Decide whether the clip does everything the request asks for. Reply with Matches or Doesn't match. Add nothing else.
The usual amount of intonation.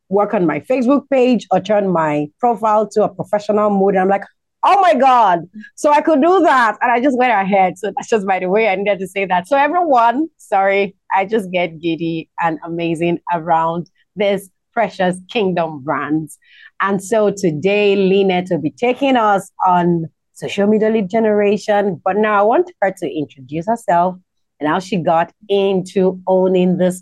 Matches